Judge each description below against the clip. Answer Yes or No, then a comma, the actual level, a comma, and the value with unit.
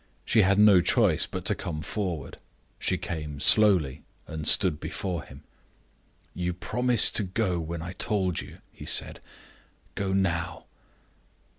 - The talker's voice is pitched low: Yes, very low, 90 Hz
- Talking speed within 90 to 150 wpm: Yes, average, 140 wpm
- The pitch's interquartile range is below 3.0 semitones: No, average, 3.7 semitones